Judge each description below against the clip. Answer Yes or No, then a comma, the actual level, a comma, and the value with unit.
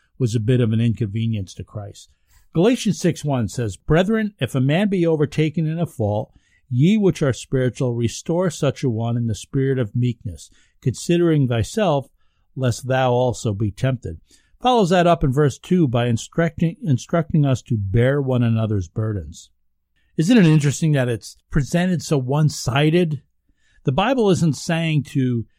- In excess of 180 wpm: No, average, 165 wpm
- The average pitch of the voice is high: No, low, 130 Hz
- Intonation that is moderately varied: No, wide, 6.2 semitones